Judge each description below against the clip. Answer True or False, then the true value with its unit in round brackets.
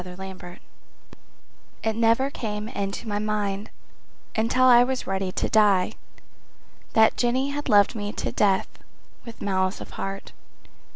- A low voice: False (210 Hz)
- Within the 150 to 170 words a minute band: False (135 wpm)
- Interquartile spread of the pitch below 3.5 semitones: True (2.9 semitones)